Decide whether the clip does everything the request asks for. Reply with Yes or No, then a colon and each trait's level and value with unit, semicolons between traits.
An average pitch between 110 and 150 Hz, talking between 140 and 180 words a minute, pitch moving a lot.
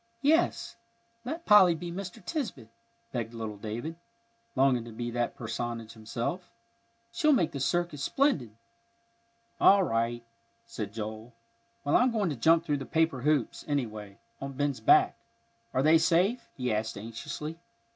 Yes: low, 135 Hz; average, 145 wpm; wide, 7.1 semitones